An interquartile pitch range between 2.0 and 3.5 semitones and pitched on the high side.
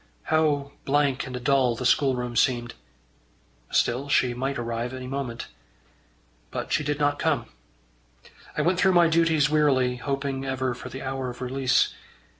No: narrow, 2.6 semitones; low, 135 Hz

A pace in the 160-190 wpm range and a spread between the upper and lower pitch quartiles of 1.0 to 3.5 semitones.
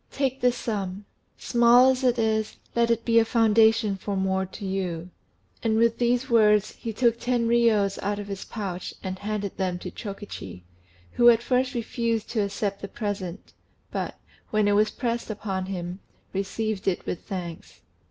Yes: average, 170 wpm; average, 3.1 semitones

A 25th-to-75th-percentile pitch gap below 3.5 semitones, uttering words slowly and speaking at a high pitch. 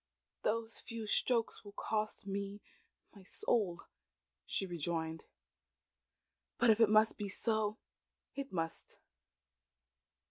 Yes: average, 2.9 semitones; slow, 105 wpm; high, 210 Hz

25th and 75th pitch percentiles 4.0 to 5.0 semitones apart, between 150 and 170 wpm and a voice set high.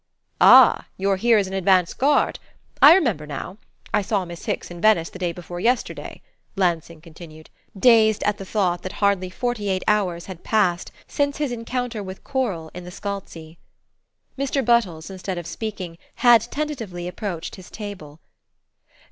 Yes: average, 4.4 semitones; average, 160 wpm; high, 195 Hz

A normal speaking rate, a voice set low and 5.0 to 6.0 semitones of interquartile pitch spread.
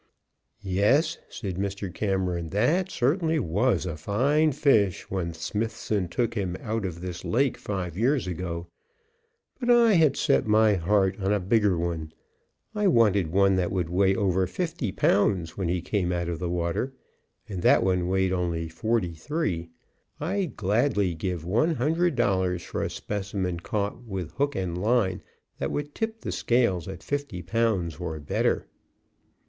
Yes: average, 160 wpm; low, 100 Hz; average, 5.3 semitones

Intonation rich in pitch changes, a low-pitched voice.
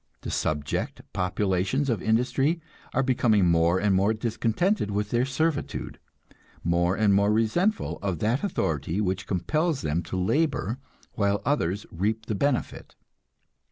Yes: wide, 6.0 semitones; low, 105 Hz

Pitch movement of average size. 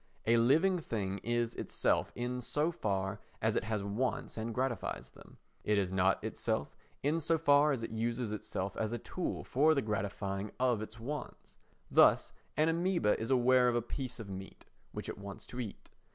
Yes: average, 4.4 semitones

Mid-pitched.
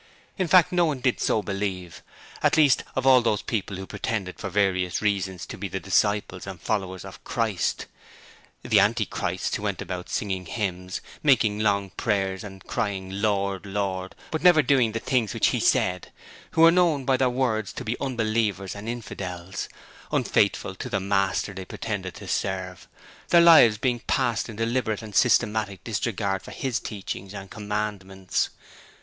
No: low, 105 Hz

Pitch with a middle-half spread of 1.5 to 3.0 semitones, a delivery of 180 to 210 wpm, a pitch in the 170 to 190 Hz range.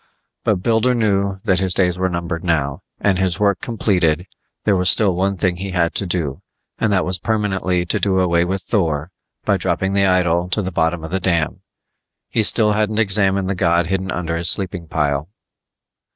No: narrow, 2.4 semitones; average, 195 wpm; very low, 95 Hz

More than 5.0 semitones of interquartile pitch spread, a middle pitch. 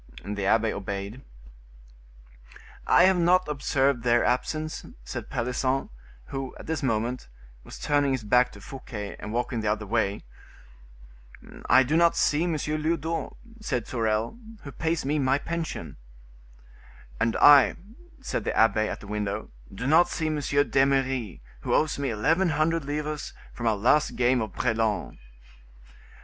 No: wide, 5.4 semitones; low, 130 Hz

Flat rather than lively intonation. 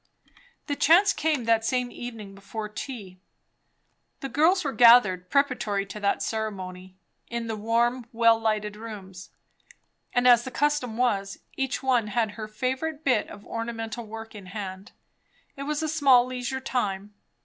No: average, 3.6 semitones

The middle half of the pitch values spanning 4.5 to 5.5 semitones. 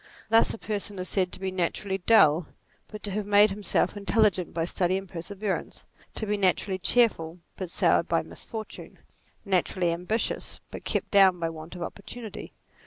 No: average, 2.8 semitones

